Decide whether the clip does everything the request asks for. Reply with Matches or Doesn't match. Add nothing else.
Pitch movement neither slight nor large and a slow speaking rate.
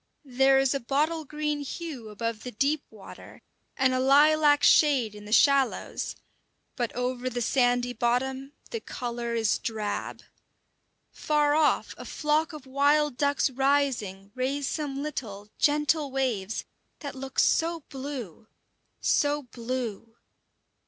Matches